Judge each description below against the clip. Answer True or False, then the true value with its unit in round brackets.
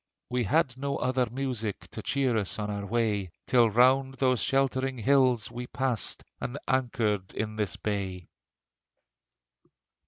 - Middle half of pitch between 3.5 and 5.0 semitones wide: True (3.8 semitones)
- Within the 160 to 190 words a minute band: False (135 wpm)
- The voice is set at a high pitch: False (120 Hz)